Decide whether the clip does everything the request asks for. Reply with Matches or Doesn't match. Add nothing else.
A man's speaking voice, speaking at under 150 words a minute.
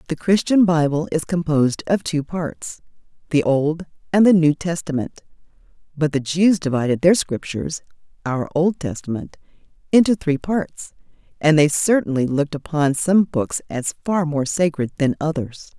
Doesn't match